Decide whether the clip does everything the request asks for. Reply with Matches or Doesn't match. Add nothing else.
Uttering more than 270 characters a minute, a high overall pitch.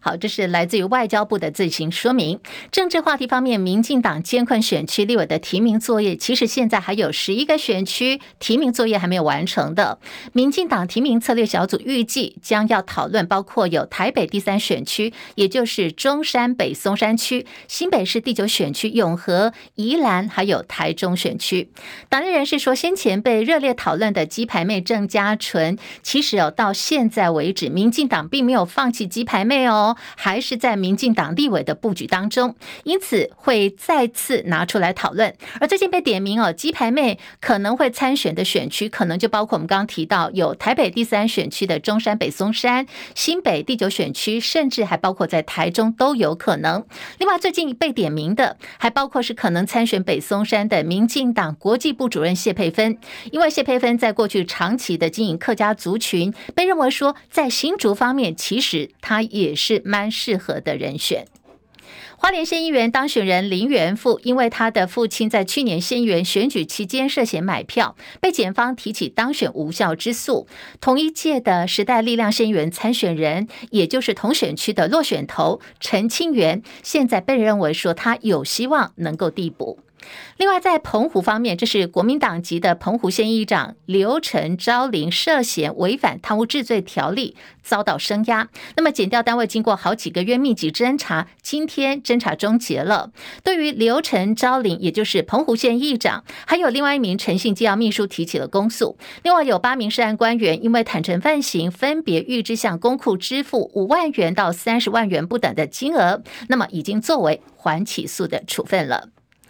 Matches